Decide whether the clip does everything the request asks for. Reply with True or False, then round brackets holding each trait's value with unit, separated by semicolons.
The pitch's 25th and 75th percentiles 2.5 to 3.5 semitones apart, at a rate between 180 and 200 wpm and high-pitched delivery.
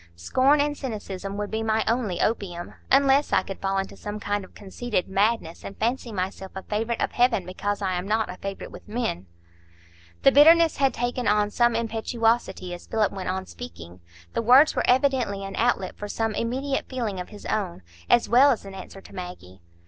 False (4.1 semitones; 195 wpm; 210 Hz)